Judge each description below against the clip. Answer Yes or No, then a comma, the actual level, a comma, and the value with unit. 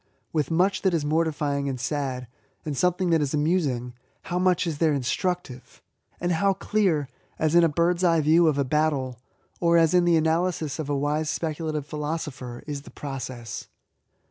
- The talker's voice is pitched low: No, medium, 155 Hz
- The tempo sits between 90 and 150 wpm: No, average, 175 wpm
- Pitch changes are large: No, average, 3.2 semitones